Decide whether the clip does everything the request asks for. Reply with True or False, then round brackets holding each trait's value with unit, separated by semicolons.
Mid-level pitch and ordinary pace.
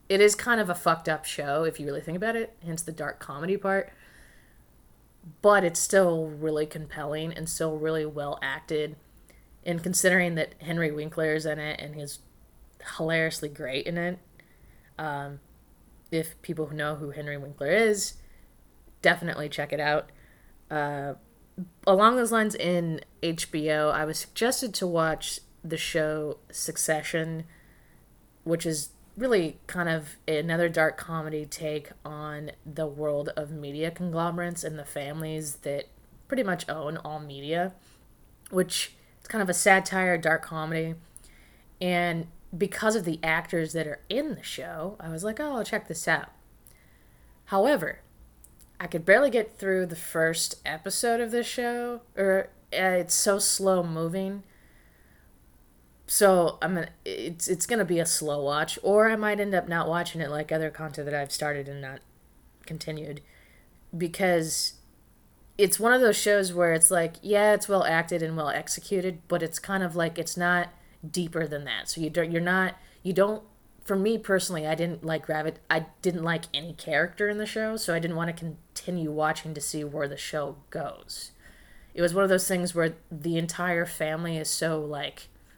True (165 Hz; 165 wpm)